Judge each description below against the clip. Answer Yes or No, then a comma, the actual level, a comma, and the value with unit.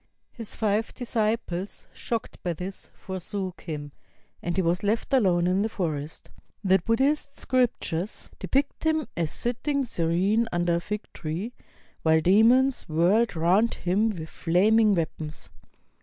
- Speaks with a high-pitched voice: Yes, high, 195 Hz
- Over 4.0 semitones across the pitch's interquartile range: Yes, average, 4.9 semitones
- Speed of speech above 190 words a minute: No, slow, 135 wpm